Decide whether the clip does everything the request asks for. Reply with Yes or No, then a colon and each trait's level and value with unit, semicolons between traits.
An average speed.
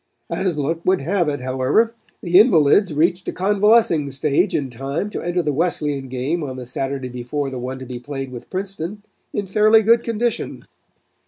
Yes: average, 180 wpm